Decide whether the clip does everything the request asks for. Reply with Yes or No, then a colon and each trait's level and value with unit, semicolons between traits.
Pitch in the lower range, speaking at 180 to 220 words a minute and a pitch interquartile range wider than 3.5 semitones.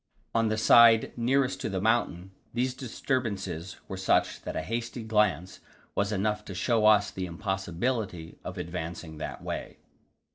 No: low, 105 Hz; average, 150 wpm; average, 4.0 semitones